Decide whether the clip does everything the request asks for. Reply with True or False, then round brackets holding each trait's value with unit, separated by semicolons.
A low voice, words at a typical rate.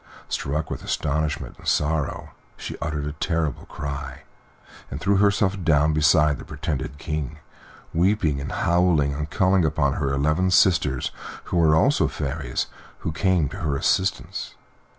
True (75 Hz; 150 wpm)